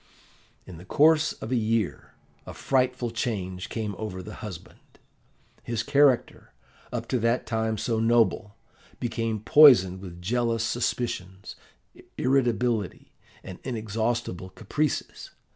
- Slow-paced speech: Yes, slow, 115 wpm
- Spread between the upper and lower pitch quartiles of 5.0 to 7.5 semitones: No, average, 3.5 semitones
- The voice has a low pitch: Yes, low, 115 Hz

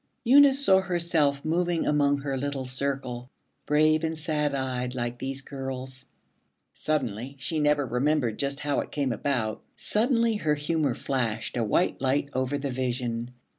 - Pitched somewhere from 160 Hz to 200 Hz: No, medium, 140 Hz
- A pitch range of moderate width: Yes, average, 3.2 semitones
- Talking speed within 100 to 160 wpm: Yes, average, 150 wpm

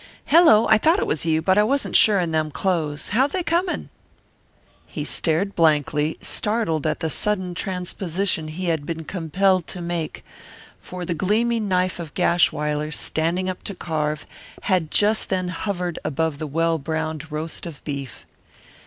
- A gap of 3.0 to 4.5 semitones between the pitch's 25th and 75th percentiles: Yes, average, 3.8 semitones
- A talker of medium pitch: Yes, medium, 170 Hz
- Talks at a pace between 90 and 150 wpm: No, average, 160 wpm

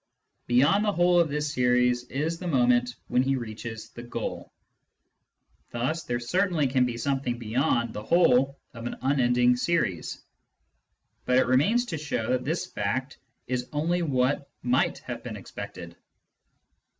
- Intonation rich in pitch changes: No, average, 3.7 semitones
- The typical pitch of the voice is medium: No, low, 130 Hz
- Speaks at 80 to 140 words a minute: No, average, 150 wpm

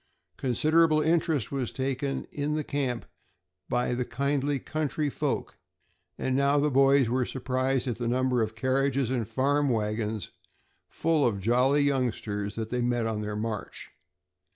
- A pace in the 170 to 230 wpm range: No, average, 150 wpm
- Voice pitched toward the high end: No, low, 130 Hz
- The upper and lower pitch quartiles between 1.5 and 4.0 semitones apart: Yes, average, 3.3 semitones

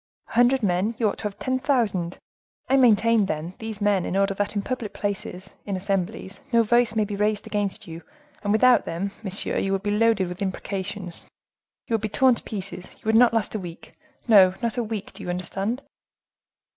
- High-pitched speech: Yes, high, 205 Hz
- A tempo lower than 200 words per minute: No, fast, 205 wpm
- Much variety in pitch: No, average, 3.0 semitones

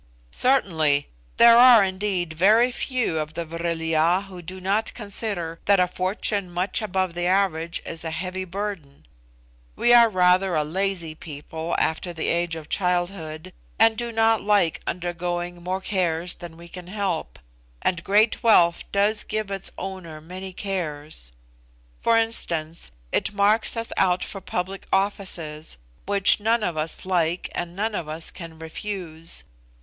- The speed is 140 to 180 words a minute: Yes, average, 155 wpm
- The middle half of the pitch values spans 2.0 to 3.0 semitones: No, average, 3.4 semitones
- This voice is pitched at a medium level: Yes, medium, 180 Hz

